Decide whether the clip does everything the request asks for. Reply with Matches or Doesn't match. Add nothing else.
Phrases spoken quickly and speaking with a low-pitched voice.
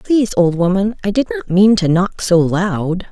Doesn't match